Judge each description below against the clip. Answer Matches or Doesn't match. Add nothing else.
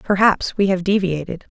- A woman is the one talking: Matches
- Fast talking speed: Doesn't match